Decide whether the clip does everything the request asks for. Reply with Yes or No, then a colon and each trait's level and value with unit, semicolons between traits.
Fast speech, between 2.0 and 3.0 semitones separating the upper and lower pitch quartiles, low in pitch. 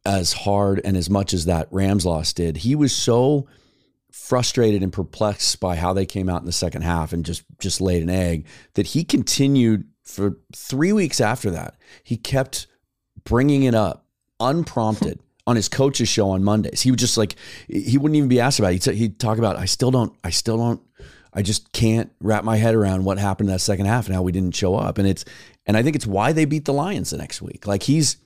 No: fast, 225 wpm; average, 5.1 semitones; low, 105 Hz